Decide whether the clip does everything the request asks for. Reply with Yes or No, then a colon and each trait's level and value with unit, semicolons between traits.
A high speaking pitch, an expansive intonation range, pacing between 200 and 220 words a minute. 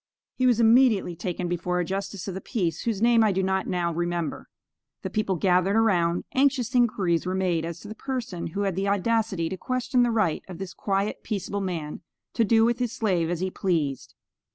No: high, 195 Hz; average, 4.2 semitones; fast, 205 wpm